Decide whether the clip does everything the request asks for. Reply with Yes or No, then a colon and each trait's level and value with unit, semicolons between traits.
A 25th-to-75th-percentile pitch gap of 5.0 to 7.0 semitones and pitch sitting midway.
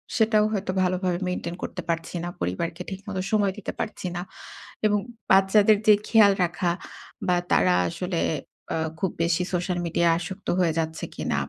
No: average, 2.7 semitones; medium, 180 Hz